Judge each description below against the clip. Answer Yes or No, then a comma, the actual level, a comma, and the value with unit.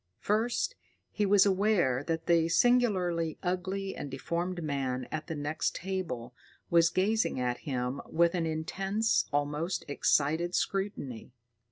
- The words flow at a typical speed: No, slow, 130 wpm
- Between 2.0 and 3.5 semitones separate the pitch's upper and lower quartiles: No, average, 4.9 semitones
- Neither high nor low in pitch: Yes, medium, 170 Hz